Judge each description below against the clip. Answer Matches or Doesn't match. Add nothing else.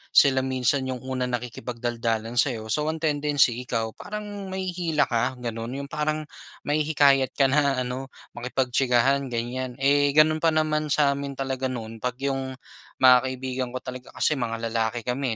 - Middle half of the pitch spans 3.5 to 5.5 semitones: Doesn't match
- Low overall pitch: Matches